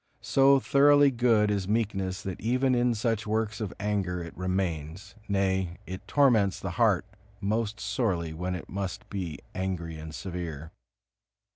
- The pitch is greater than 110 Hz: No, low, 100 Hz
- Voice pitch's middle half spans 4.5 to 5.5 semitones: No, average, 3.9 semitones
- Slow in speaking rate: No, average, 145 wpm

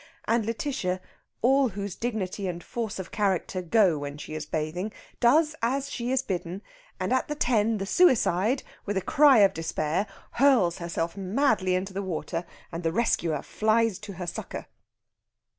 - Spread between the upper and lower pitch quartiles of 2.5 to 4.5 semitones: No, average, 5.1 semitones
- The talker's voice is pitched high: Yes, high, 200 Hz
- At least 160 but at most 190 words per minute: Yes, average, 165 wpm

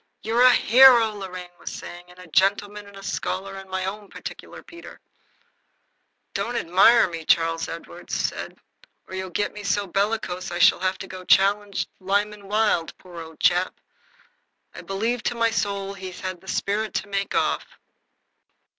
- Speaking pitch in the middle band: No, high, 195 Hz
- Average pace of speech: Yes, average, 165 wpm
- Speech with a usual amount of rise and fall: No, narrow, 2.2 semitones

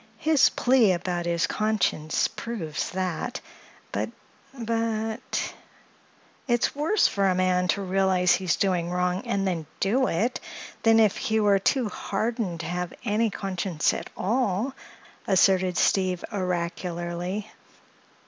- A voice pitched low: No, high, 190 Hz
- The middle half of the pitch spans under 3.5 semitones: No, average, 3.8 semitones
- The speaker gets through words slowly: Yes, slow, 120 wpm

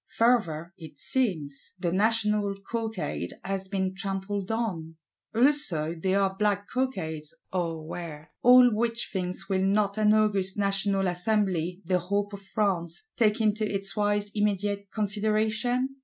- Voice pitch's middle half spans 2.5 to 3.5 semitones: Yes, average, 3.0 semitones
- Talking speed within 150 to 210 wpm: No, slow, 135 wpm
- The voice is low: No, high, 200 Hz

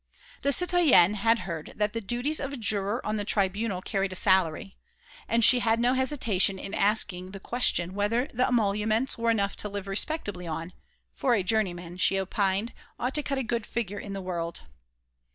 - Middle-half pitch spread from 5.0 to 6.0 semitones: No, average, 3.6 semitones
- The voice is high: Yes, high, 205 Hz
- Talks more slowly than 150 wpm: No, average, 190 wpm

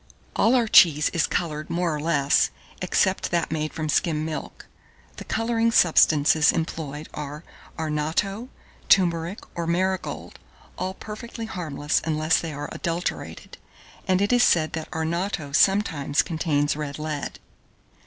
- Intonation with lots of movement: No, average, 3.6 semitones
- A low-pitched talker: No, medium, 165 Hz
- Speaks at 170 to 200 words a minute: No, slow, 135 wpm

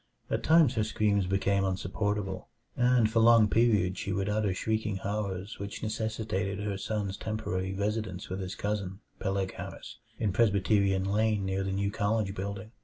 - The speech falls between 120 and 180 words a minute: Yes, average, 160 wpm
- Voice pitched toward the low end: Yes, low, 100 Hz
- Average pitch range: No, narrow, 2.1 semitones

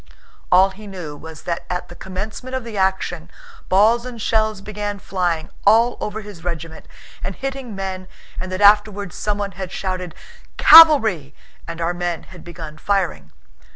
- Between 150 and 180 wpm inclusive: Yes, average, 155 wpm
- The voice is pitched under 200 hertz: Yes, high, 190 Hz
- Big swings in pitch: No, average, 3.3 semitones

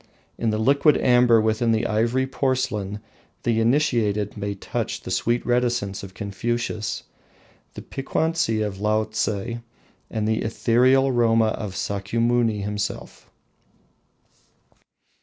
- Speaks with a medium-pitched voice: No, low, 115 Hz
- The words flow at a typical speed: No, slow, 110 wpm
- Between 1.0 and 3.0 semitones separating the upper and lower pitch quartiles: Yes, narrow, 2.5 semitones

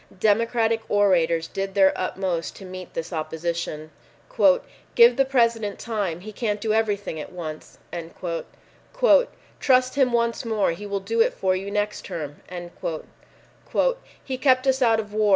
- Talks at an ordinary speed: Yes, average, 145 wpm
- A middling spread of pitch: Yes, average, 4.1 semitones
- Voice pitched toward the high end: Yes, high, 205 Hz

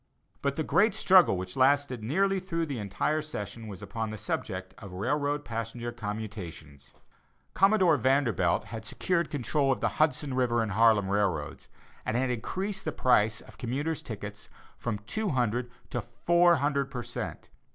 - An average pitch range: No, wide, 5.7 semitones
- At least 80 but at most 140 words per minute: No, average, 160 wpm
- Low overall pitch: Yes, low, 125 Hz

